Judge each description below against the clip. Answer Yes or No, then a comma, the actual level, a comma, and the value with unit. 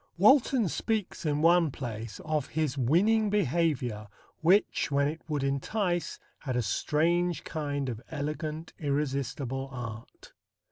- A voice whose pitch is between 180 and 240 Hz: No, medium, 150 Hz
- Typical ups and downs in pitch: Yes, average, 4.4 semitones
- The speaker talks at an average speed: No, slow, 125 wpm